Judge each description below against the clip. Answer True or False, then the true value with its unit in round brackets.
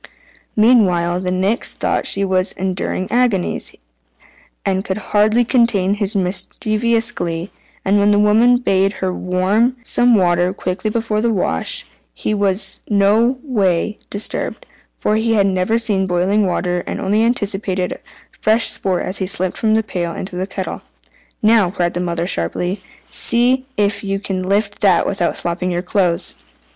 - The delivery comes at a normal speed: True (155 wpm)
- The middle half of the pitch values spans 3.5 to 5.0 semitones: False (3.0 semitones)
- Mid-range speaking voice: False (195 Hz)